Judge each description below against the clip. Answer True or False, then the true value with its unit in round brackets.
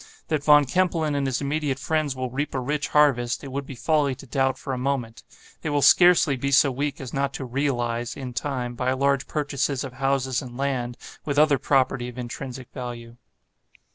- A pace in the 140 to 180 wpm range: False (200 wpm)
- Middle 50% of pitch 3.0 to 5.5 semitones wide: False (2.4 semitones)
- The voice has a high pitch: False (135 Hz)